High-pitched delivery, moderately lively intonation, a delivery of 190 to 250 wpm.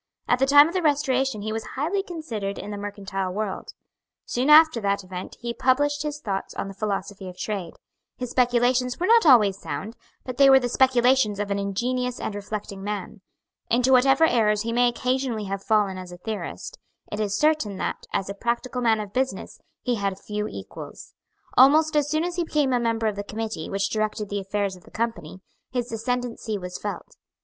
Yes: high, 225 Hz; average, 4.4 semitones; average, 200 wpm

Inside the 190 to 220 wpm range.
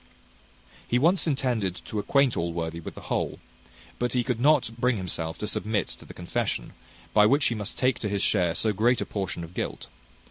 Yes: average, 200 wpm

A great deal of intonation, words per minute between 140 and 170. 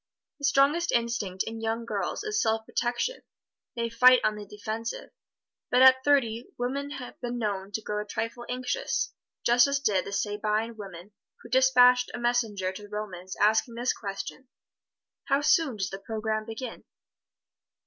No: average, 3.2 semitones; average, 160 wpm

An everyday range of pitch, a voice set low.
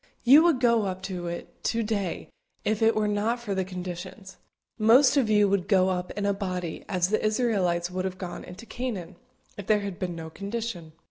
No: average, 3.4 semitones; high, 200 Hz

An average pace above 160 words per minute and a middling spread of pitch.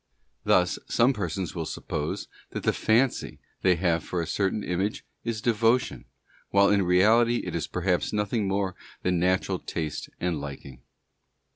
No: average, 150 wpm; average, 3.4 semitones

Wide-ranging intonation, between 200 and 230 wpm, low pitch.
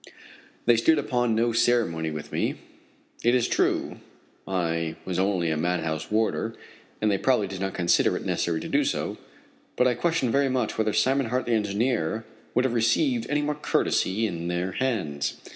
No: wide, 6.0 semitones; average, 175 wpm; low, 110 Hz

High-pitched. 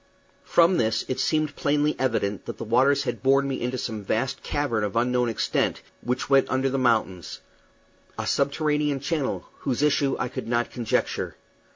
No: low, 130 Hz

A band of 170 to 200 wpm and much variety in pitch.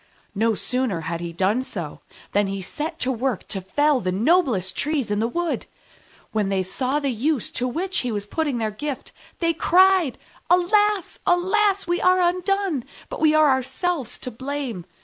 Yes: average, 175 wpm; wide, 8.4 semitones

